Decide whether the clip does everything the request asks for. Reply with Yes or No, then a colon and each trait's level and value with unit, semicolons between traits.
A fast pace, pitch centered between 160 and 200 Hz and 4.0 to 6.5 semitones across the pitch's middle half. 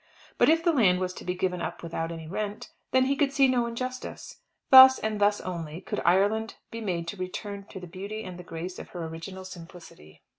Yes: fast, 220 wpm; high, 190 Hz; average, 4.3 semitones